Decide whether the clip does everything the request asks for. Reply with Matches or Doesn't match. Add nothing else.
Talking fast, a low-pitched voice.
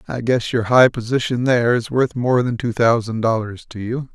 Matches